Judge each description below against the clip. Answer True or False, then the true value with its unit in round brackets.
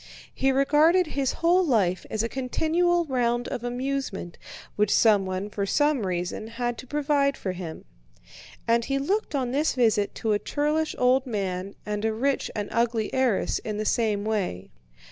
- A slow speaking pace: False (165 wpm)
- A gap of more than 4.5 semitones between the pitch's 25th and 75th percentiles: True (5.1 semitones)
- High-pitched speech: True (240 Hz)